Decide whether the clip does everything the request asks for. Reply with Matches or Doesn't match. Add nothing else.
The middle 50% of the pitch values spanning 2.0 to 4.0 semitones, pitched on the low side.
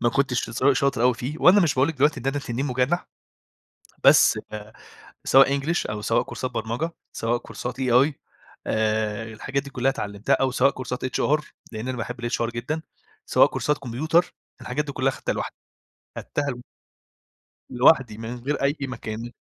Matches